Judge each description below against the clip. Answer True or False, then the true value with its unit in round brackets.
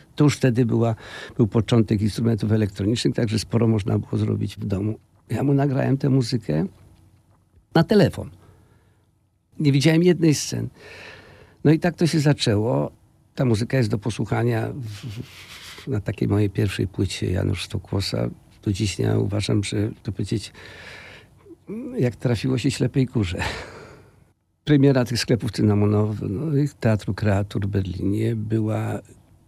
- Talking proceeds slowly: False (140 wpm)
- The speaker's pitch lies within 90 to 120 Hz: True (110 Hz)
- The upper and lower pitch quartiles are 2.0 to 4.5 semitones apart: True (3.6 semitones)